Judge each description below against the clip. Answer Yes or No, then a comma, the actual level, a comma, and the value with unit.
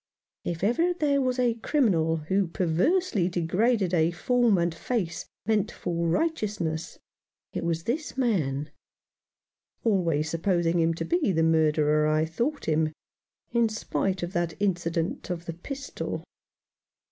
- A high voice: No, medium, 175 Hz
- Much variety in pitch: Yes, wide, 6.2 semitones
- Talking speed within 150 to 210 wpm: No, slow, 135 wpm